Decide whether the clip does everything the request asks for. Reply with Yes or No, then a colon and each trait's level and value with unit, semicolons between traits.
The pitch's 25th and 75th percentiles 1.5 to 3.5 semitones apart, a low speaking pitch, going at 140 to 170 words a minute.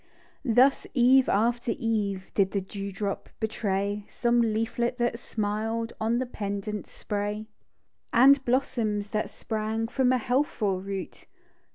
No: average, 2.8 semitones; high, 220 Hz; average, 150 wpm